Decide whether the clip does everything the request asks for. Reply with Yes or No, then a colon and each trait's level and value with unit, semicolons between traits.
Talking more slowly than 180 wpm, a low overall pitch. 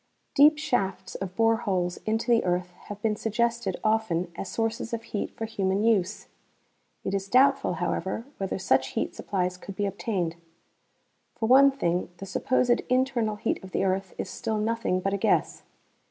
No: average, 170 wpm; high, 210 Hz